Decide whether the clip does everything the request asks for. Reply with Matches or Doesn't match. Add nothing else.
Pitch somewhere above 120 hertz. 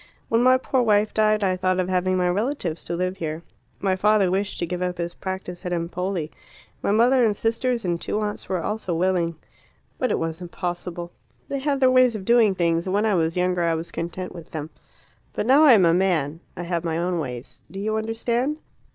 Matches